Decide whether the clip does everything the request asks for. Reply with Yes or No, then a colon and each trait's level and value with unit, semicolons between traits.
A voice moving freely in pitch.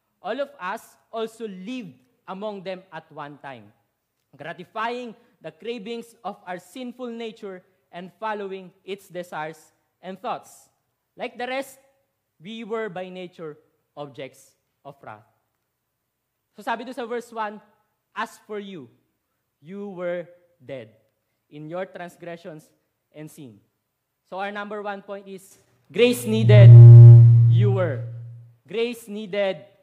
Yes: wide, 8.0 semitones